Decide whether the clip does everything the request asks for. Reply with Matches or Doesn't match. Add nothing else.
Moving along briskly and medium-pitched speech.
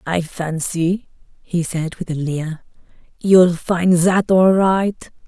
Doesn't match